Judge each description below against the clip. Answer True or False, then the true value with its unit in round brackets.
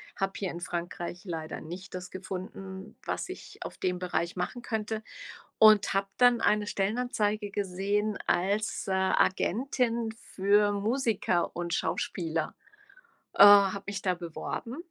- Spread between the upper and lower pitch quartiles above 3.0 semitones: False (2.7 semitones)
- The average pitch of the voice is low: False (195 Hz)